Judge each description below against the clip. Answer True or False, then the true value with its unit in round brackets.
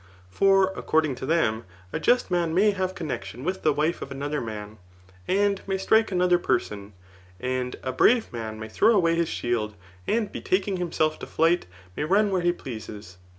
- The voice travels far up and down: True (7.9 semitones)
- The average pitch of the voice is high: False (165 Hz)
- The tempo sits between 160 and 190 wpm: True (185 wpm)